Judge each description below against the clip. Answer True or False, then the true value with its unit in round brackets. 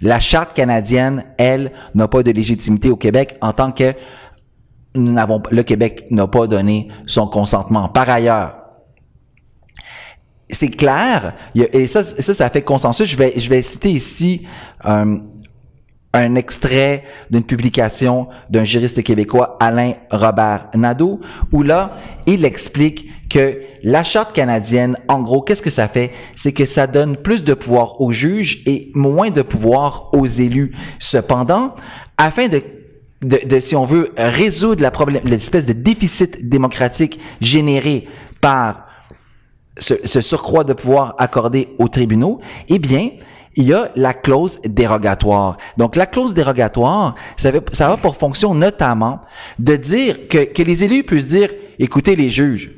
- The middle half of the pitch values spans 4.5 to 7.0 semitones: False (3.9 semitones)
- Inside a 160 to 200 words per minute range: False (150 wpm)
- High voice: False (130 Hz)